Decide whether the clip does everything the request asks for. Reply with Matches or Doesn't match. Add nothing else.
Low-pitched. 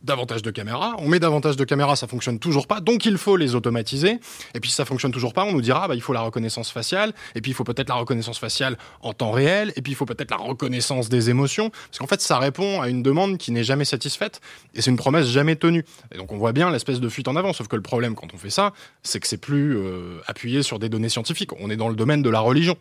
Matches